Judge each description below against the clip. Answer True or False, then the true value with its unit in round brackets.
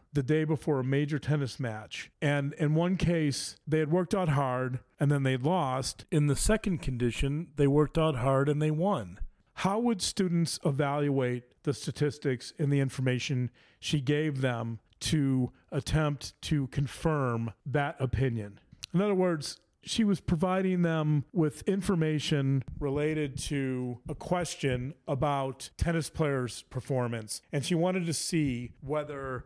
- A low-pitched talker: False (145 Hz)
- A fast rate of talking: False (145 wpm)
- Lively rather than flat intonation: False (3.5 semitones)